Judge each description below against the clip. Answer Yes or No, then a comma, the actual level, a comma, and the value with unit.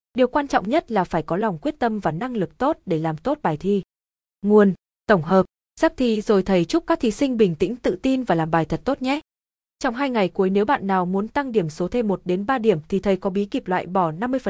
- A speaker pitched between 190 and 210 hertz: Yes, high, 205 Hz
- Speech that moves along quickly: Yes, fast, 265 wpm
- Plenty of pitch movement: Yes, wide, 6.0 semitones